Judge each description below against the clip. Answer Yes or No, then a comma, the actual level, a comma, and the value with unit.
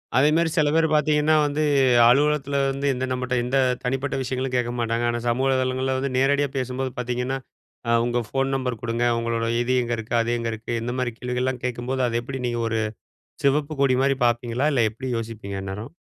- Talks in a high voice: No, low, 130 Hz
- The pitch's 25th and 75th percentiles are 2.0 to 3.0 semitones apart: Yes, narrow, 2.4 semitones